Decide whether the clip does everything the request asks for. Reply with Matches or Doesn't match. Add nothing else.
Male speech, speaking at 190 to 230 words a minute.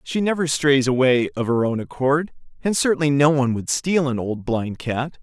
Matches